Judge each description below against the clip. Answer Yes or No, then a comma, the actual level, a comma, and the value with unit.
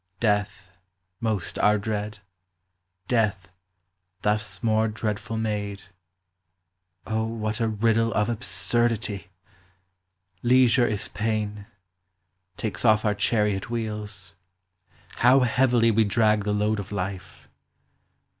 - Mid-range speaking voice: No, low, 110 Hz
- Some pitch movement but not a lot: No, narrow, 1.8 semitones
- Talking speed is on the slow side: Yes, slow, 100 wpm